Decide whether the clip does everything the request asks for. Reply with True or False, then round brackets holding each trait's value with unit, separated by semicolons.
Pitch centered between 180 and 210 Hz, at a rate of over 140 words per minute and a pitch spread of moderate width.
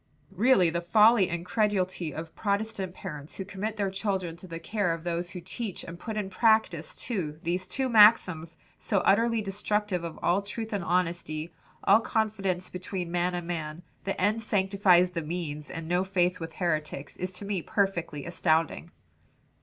True (185 Hz; 170 wpm; 3.3 semitones)